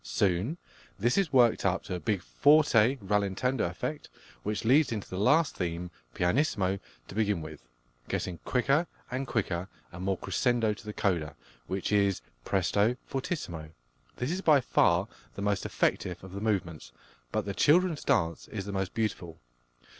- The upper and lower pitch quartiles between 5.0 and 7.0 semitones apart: Yes, wide, 5.5 semitones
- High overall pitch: No, low, 100 Hz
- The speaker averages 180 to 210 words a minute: No, average, 160 wpm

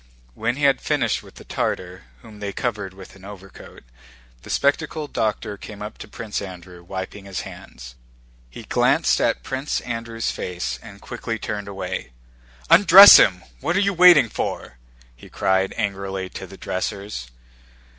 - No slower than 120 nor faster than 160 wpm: Yes, average, 155 wpm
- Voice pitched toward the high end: No, low, 105 Hz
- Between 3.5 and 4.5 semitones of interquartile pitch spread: Yes, average, 4.1 semitones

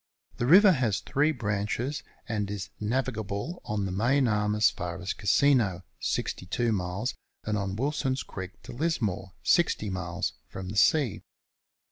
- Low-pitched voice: Yes, low, 105 Hz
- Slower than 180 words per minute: Yes, average, 145 wpm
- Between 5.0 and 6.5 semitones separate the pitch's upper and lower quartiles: Yes, average, 5.3 semitones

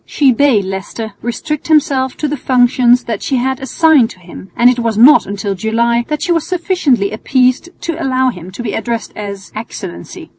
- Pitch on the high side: Yes, high, 245 Hz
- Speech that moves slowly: No, average, 190 wpm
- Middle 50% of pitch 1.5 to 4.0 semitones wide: No, average, 4.5 semitones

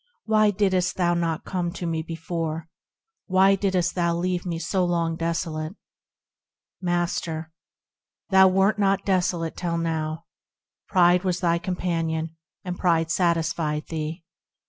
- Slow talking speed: Yes, slow, 125 wpm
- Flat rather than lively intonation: Yes, narrow, 2.0 semitones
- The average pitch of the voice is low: No, medium, 170 Hz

